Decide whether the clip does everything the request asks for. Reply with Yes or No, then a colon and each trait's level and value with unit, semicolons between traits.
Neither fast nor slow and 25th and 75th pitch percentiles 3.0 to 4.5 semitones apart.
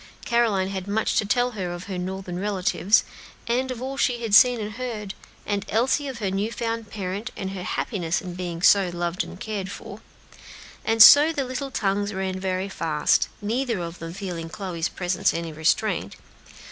Yes: average, 180 wpm; average, 4.0 semitones